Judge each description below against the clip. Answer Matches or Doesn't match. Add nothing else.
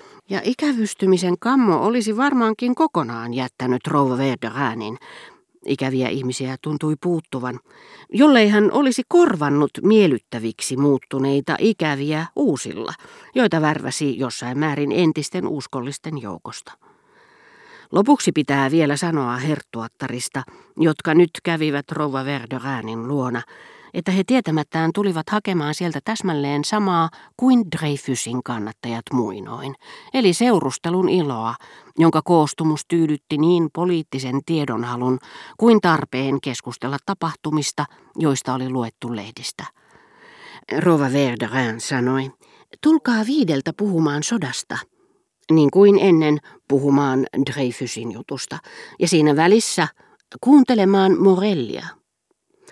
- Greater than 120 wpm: Doesn't match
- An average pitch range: Doesn't match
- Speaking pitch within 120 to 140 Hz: Doesn't match